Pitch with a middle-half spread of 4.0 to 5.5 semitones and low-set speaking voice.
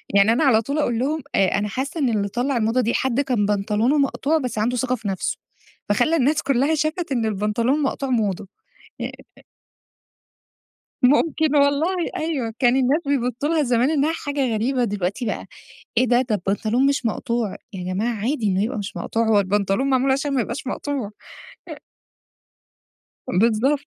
No: average, 4.6 semitones; very high, 250 Hz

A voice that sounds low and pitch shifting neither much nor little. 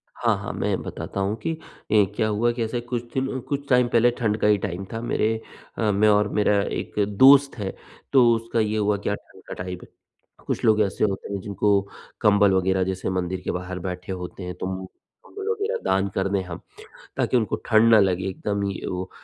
Yes: low, 105 Hz; average, 3.4 semitones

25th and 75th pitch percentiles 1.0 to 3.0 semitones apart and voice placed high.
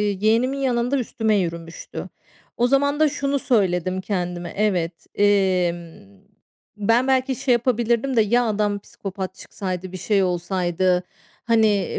No: average, 4.8 semitones; high, 205 Hz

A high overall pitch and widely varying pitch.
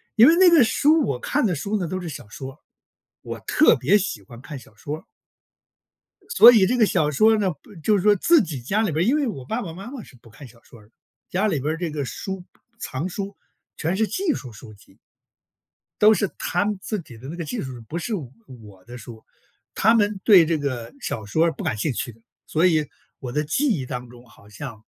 No: medium, 165 Hz; wide, 8.9 semitones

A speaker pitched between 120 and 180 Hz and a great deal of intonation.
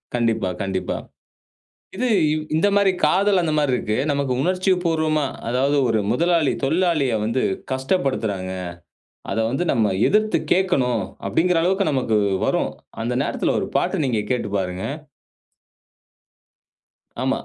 Yes: medium, 140 Hz; wide, 7.6 semitones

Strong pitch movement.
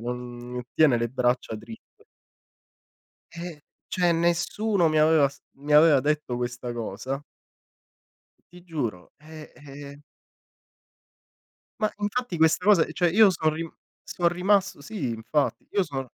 Yes: wide, 5.8 semitones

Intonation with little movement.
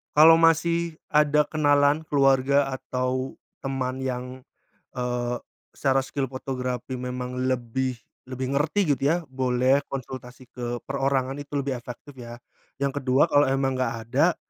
Yes: narrow, 2.0 semitones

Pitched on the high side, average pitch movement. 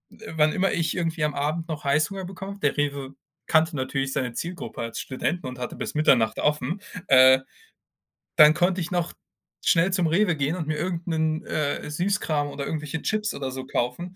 No: medium, 155 Hz; average, 3.9 semitones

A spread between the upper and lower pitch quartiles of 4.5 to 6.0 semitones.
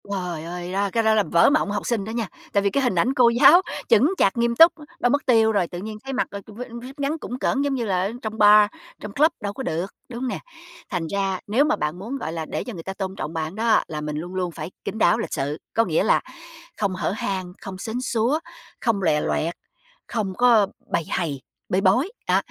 Yes: average, 4.8 semitones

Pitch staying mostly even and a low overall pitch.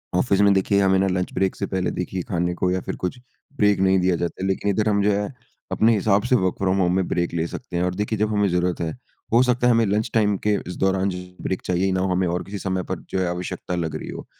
Yes: narrow, 2.2 semitones; very low, 95 Hz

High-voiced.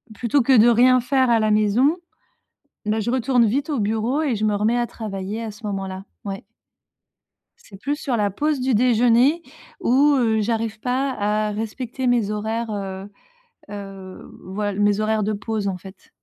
Yes: high, 220 Hz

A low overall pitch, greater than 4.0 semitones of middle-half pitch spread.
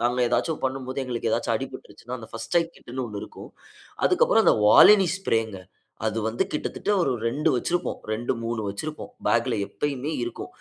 Yes: low, 125 Hz; average, 4.4 semitones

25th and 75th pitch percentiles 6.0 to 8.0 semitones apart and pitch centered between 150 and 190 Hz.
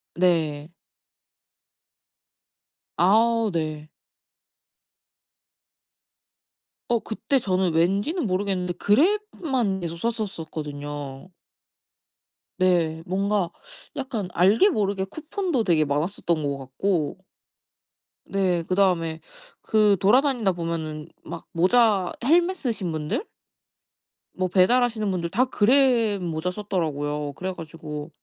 No: average, 5.3 semitones; medium, 185 Hz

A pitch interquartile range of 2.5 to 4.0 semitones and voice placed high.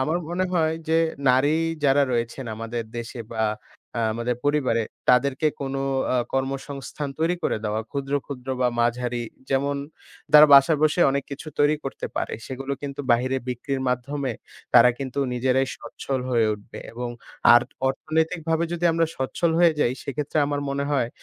No: average, 3.1 semitones; low, 135 Hz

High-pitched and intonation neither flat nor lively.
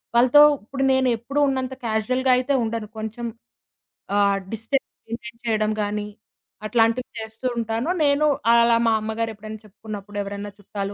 Yes: high, 225 Hz; average, 3.0 semitones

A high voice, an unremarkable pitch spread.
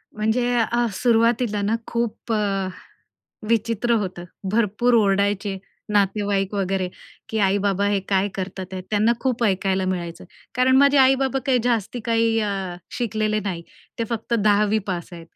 Yes: high, 210 Hz; average, 3.1 semitones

